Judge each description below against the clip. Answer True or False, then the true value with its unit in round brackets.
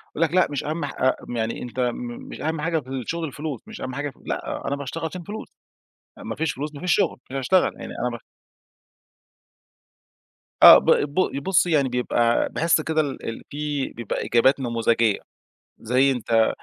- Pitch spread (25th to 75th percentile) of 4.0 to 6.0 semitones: True (4.6 semitones)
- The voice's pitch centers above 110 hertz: True (140 Hz)